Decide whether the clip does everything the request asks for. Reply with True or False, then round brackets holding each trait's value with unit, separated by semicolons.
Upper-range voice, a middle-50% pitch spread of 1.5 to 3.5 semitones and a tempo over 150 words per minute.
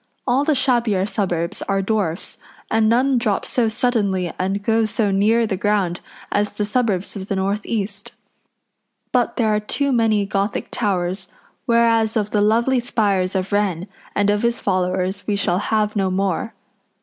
True (205 Hz; 2.8 semitones; 165 wpm)